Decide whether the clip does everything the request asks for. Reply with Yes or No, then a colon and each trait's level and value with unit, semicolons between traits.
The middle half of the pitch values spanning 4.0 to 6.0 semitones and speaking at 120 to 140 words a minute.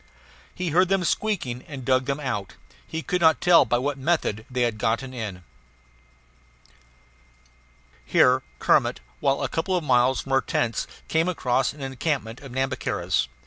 No: average, 4.7 semitones; average, 155 wpm